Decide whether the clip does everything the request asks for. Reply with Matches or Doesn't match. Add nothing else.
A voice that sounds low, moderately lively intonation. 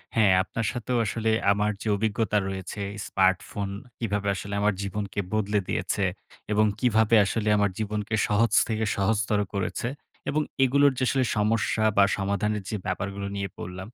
Doesn't match